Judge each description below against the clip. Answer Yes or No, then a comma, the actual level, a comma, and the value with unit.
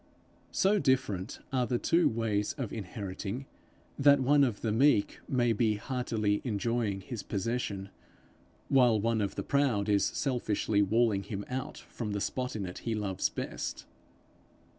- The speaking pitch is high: No, low, 115 Hz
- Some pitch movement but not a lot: Yes, average, 3.9 semitones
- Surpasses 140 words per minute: Yes, average, 150 wpm